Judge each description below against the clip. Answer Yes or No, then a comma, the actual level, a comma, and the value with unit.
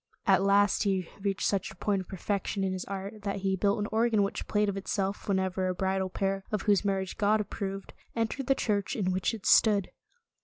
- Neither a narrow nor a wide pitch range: No, narrow, 1.4 semitones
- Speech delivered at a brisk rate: Yes, fast, 220 wpm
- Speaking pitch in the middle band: No, high, 195 Hz